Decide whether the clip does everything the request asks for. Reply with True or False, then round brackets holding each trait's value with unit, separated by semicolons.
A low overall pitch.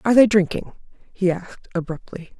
False (185 Hz)